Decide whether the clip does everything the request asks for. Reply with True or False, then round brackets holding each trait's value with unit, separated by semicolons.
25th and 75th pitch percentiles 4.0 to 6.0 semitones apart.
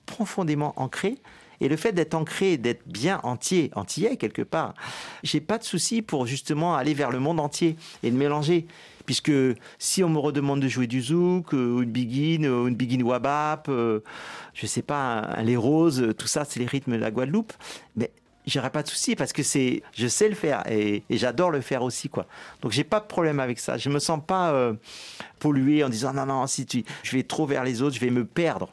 True (4.6 semitones)